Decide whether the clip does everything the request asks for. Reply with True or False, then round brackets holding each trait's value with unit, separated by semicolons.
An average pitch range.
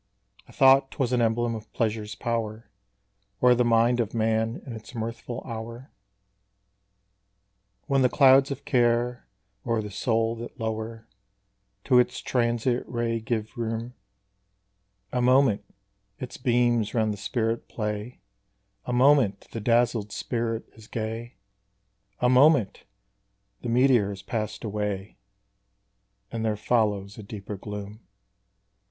False (2.0 semitones)